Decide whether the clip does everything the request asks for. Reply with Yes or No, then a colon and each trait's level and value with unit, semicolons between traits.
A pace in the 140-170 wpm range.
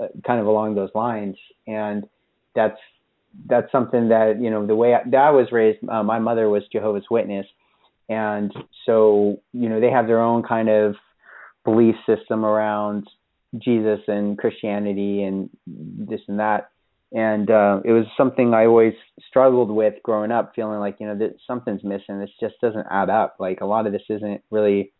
No: average, 180 wpm